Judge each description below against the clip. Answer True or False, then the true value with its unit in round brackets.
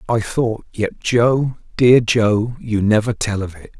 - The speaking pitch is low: True (110 Hz)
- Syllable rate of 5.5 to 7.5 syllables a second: False (3.7 syllables/s)